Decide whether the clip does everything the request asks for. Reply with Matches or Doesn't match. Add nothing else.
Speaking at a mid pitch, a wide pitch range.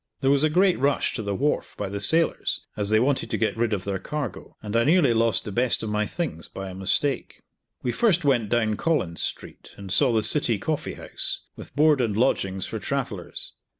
Doesn't match